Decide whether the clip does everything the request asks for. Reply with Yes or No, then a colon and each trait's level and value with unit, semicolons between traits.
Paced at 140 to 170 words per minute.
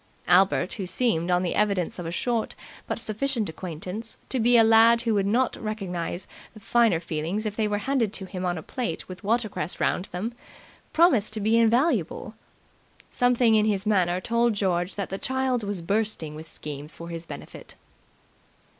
No: average, 180 wpm